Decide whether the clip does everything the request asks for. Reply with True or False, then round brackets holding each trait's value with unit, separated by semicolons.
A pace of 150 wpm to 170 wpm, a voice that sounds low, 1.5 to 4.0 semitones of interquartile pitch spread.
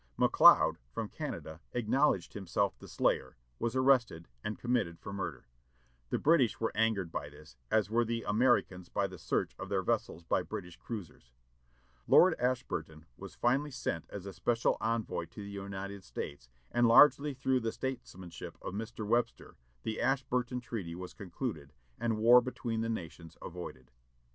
False (160 wpm; 110 Hz; 5.5 semitones)